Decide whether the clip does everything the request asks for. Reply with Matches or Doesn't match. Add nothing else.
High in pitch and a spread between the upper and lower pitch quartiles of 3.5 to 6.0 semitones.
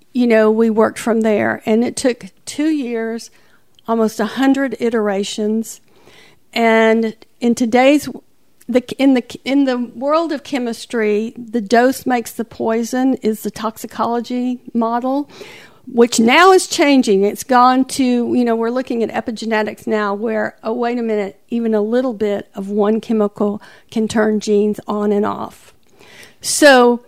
Doesn't match